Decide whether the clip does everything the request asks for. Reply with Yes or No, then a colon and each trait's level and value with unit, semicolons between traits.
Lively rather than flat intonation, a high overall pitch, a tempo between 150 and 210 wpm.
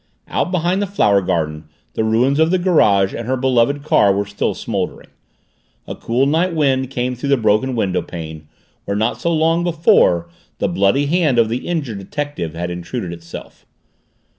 No: wide, 7.6 semitones; low, 125 Hz; average, 170 wpm